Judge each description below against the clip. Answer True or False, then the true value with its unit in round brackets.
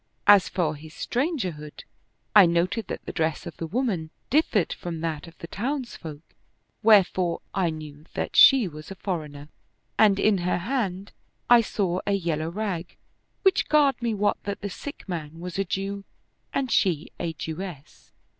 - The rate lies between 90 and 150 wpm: False (165 wpm)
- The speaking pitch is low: False (185 Hz)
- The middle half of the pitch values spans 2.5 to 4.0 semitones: False (4.6 semitones)